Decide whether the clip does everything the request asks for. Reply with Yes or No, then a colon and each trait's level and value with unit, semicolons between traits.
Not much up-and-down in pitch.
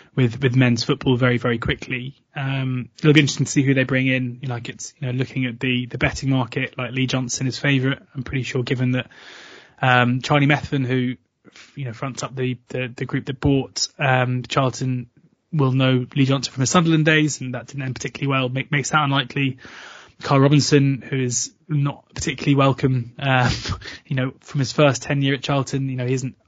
Yes: narrow, 1.9 semitones